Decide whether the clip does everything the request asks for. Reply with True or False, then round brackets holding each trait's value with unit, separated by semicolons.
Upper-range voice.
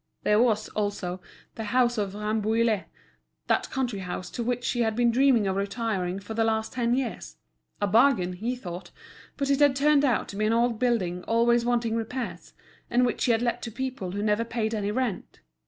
True (230 Hz)